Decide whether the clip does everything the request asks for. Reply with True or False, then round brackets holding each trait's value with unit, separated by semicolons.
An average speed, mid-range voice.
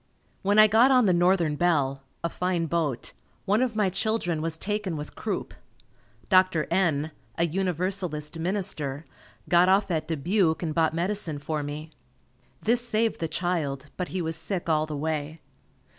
True (160 wpm; 170 Hz)